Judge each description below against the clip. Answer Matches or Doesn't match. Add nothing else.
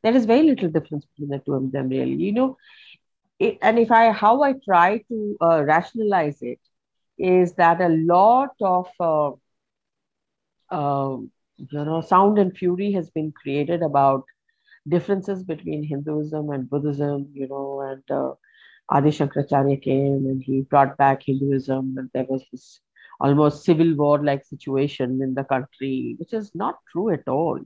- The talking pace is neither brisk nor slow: Matches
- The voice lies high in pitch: Doesn't match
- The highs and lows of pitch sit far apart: Doesn't match